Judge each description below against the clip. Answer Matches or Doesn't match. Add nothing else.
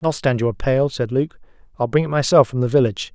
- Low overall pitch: Matches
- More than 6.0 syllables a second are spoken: Matches